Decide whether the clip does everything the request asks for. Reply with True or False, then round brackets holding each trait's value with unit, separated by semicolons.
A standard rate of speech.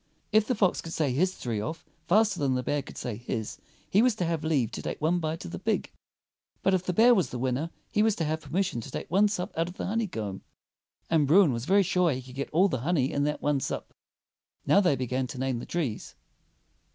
False (250 wpm)